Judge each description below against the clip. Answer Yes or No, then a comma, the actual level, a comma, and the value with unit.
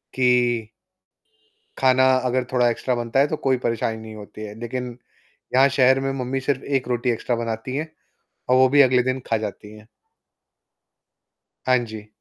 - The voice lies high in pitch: No, low, 125 Hz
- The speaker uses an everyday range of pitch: No, narrow, 2.1 semitones